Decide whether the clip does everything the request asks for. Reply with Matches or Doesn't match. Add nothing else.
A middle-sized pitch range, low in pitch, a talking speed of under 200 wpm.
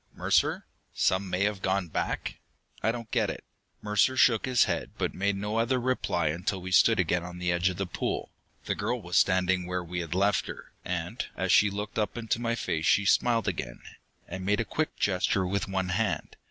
Doesn't match